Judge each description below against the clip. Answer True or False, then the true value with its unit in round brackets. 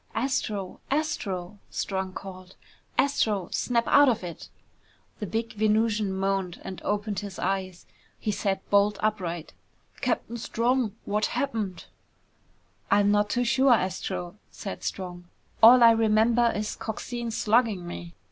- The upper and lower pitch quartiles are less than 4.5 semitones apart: True (3.3 semitones)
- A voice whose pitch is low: False (210 Hz)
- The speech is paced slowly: True (130 wpm)